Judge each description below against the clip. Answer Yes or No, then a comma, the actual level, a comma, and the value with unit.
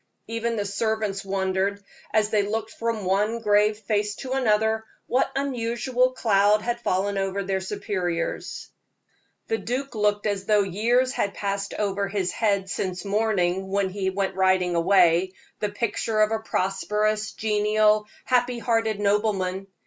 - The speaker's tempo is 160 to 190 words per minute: No, average, 145 wpm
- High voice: Yes, high, 210 Hz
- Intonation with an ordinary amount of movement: No, narrow, 2.2 semitones